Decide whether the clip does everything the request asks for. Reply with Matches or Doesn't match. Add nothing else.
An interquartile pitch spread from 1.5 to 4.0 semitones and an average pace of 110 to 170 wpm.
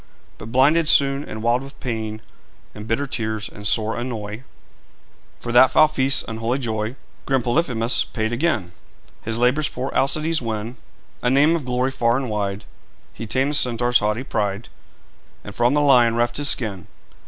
Matches